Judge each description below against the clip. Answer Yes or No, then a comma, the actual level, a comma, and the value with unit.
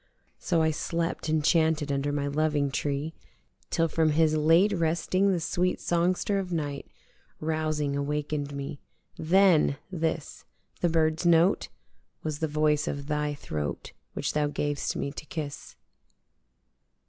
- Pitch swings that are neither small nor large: No, narrow, 2.2 semitones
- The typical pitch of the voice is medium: Yes, medium, 155 Hz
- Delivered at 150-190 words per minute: No, slow, 135 wpm